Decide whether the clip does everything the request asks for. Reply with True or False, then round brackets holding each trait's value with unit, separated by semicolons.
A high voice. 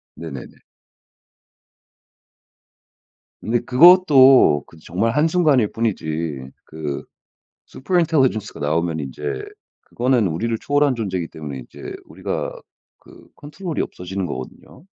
False (110 Hz)